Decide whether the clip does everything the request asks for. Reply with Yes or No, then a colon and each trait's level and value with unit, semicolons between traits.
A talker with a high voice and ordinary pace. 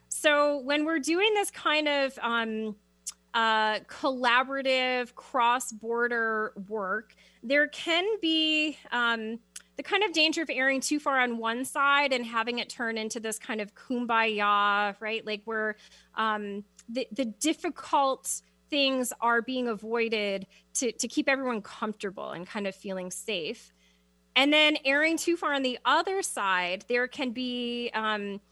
Yes: high, 240 Hz; average, 150 wpm